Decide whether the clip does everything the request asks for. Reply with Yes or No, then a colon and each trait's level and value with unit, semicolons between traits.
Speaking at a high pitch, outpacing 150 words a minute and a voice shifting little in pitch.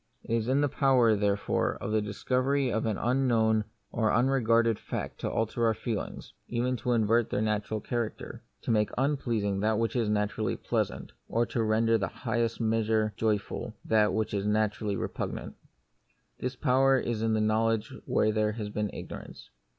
No: low, 110 Hz; average, 180 wpm; narrow, 1.8 semitones